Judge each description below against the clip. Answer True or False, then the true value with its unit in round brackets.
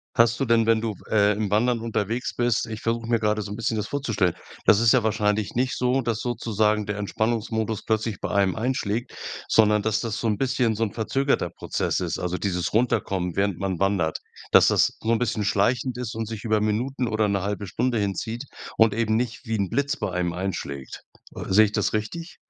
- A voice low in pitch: True (110 Hz)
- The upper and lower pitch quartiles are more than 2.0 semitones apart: True (2.4 semitones)